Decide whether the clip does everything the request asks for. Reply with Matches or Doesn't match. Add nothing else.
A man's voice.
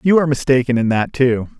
Matches